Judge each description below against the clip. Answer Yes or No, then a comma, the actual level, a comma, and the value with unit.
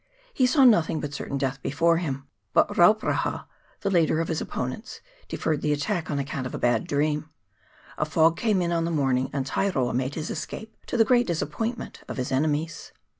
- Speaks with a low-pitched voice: No, medium, 155 Hz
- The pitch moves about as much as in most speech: Yes, average, 4.0 semitones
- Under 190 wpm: No, average, 195 wpm